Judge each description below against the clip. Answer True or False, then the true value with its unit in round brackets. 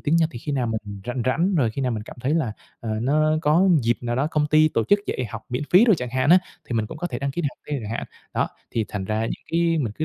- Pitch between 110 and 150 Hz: True (135 Hz)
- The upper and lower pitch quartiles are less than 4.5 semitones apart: False (5.1 semitones)